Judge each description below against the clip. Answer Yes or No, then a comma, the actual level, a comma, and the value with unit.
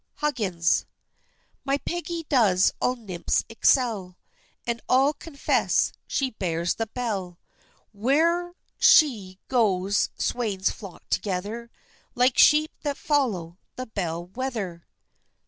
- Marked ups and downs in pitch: Yes, wide, 6.5 semitones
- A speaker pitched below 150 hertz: No, high, 225 Hz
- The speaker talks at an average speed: No, slow, 105 wpm